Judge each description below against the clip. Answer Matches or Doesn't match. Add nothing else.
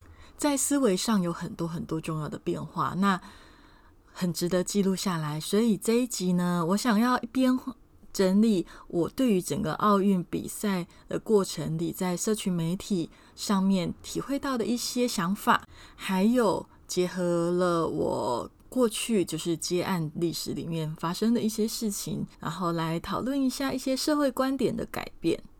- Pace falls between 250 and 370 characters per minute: Doesn't match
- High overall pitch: Matches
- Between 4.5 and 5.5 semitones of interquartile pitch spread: Matches